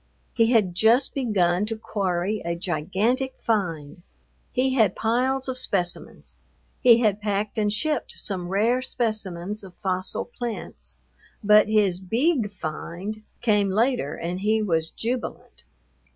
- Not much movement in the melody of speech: No, average, 4.2 semitones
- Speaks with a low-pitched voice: No, high, 210 Hz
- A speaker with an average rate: No, slow, 130 wpm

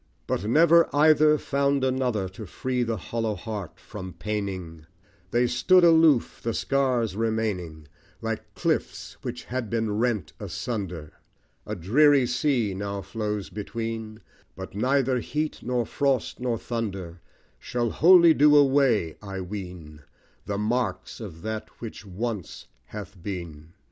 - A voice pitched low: Yes, low, 110 Hz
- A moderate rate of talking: No, slow, 130 wpm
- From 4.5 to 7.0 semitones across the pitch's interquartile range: Yes, average, 4.9 semitones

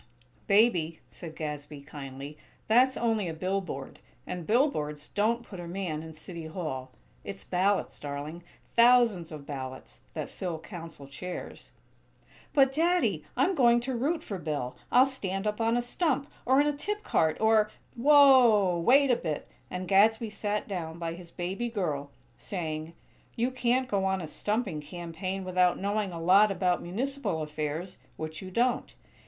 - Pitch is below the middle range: No, medium, 185 Hz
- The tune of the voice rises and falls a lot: Yes, wide, 6.7 semitones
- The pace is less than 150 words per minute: No, average, 160 wpm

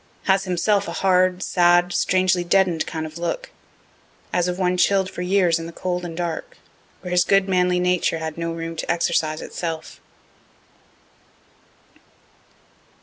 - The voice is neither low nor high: Yes, medium, 180 Hz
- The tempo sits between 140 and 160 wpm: Yes, average, 150 wpm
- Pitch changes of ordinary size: No, narrow, 1.8 semitones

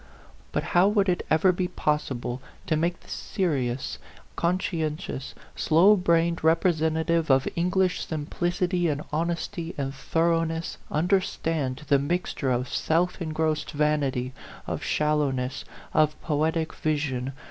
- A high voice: No, medium, 160 Hz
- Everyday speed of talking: No, slow, 125 wpm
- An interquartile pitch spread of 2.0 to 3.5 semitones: Yes, average, 2.8 semitones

